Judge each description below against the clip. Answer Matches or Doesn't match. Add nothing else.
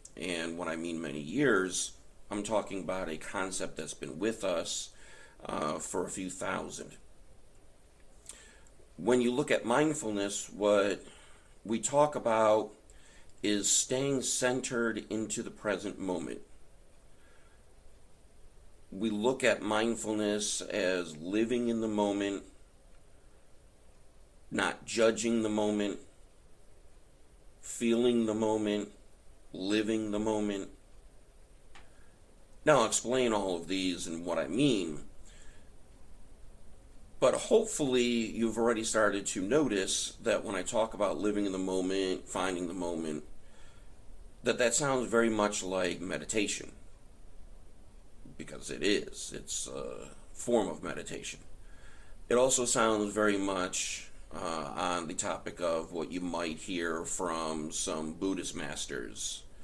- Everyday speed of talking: Doesn't match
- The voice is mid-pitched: Doesn't match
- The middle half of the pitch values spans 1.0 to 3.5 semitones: Doesn't match